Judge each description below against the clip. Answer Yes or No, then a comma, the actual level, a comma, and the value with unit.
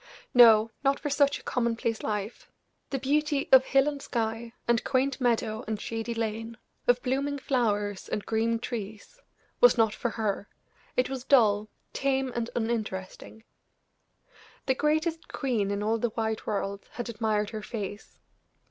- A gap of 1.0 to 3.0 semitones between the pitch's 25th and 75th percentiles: No, average, 3.5 semitones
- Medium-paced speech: Yes, average, 150 wpm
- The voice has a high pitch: Yes, high, 230 Hz